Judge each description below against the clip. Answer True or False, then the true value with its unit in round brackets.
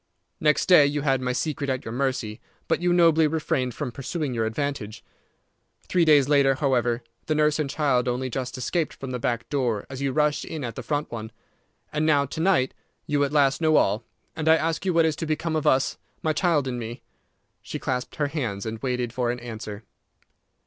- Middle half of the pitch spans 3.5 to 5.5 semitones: True (3.8 semitones)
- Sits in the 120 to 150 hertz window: True (140 Hz)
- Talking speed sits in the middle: False (210 wpm)